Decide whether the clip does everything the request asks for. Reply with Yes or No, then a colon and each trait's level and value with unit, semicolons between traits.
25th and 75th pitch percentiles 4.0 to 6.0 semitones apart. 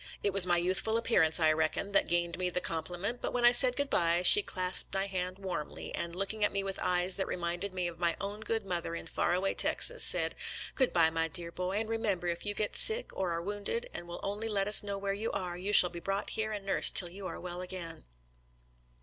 No: average, 2.9 semitones